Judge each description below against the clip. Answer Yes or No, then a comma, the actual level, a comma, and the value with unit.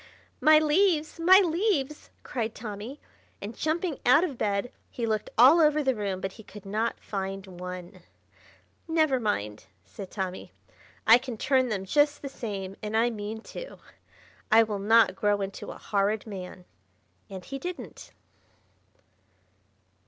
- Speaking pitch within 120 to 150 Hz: No, high, 225 Hz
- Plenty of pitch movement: Yes, wide, 6.7 semitones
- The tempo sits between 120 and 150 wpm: Yes, average, 145 wpm